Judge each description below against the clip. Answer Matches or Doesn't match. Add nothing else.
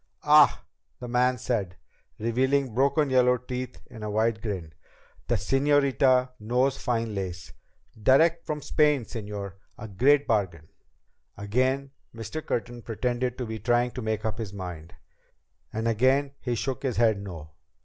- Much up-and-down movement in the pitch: Doesn't match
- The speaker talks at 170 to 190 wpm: Doesn't match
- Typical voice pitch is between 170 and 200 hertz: Doesn't match